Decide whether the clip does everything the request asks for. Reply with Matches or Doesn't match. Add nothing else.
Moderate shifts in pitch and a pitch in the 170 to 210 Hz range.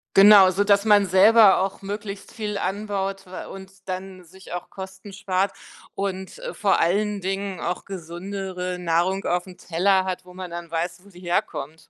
Doesn't match